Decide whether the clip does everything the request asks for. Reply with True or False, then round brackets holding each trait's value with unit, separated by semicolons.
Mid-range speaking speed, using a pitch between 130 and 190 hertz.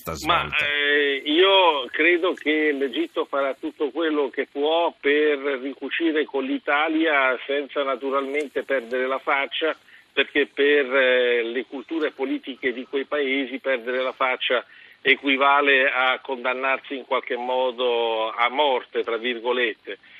True (125 wpm; 140 Hz)